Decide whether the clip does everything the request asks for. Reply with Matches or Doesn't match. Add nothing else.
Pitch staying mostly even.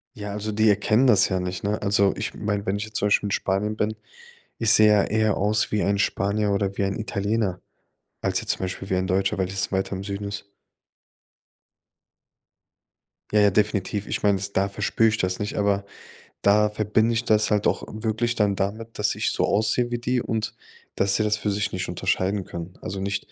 Matches